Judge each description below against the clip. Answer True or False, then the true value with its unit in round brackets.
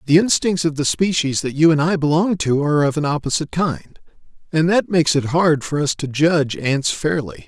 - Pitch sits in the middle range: True (155 Hz)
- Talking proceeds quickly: True (215 wpm)